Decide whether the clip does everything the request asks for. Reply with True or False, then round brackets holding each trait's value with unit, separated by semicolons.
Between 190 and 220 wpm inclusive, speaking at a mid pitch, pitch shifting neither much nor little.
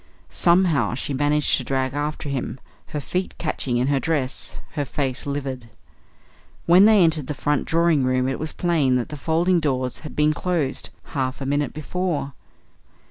False (170 wpm; 145 Hz; 3.5 semitones)